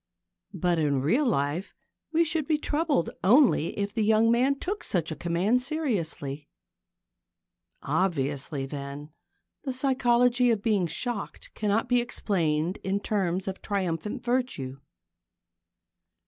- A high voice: Yes, high, 200 Hz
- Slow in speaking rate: Yes, slow, 120 wpm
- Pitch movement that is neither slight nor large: No, wide, 7.5 semitones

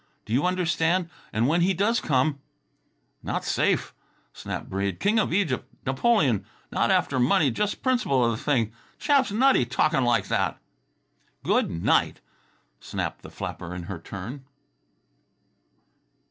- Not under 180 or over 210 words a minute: No, slow, 135 wpm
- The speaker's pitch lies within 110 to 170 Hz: Yes, medium, 140 Hz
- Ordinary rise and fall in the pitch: No, wide, 8.3 semitones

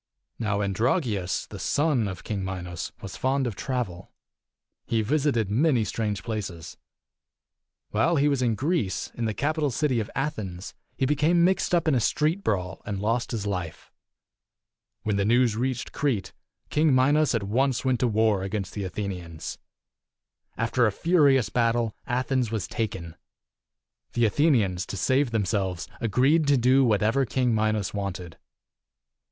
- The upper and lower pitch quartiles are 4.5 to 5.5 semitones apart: Yes, average, 5.1 semitones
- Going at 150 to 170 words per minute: Yes, average, 155 wpm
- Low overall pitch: Yes, low, 115 Hz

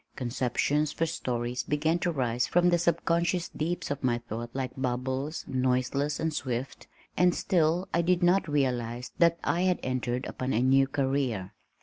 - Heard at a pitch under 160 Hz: Yes, low, 135 Hz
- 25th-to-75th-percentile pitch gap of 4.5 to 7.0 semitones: Yes, average, 5.0 semitones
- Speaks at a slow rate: No, average, 160 wpm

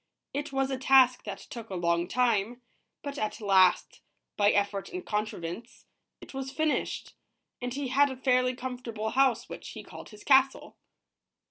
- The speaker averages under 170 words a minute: Yes, average, 160 wpm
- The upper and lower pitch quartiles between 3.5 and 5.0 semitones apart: Yes, average, 4.2 semitones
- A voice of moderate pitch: No, high, 245 Hz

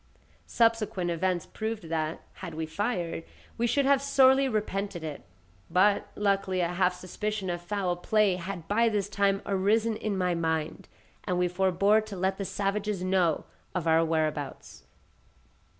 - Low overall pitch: No, high, 190 Hz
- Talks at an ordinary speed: Yes, average, 150 wpm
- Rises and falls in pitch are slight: No, average, 3.3 semitones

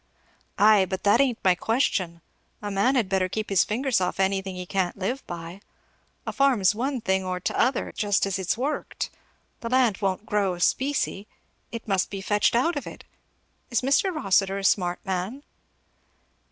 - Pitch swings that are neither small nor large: Yes, average, 4.2 semitones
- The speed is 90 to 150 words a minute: No, average, 170 wpm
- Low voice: No, high, 200 Hz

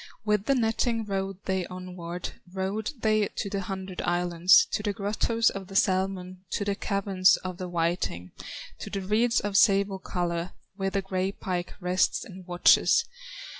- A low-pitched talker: No, high, 190 Hz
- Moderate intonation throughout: No, narrow, 1.9 semitones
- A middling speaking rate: Yes, average, 165 wpm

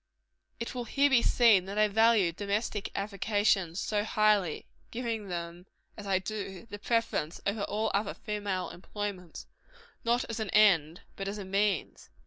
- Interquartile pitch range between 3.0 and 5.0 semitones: No, narrow, 2.5 semitones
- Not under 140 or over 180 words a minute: Yes, average, 155 wpm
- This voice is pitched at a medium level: No, high, 205 Hz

